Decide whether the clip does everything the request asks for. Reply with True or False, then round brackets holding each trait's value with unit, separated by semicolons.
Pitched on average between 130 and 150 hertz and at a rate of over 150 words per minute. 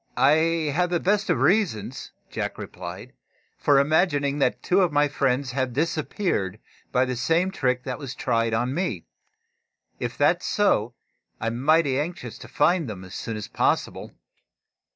True (140 Hz; 160 wpm)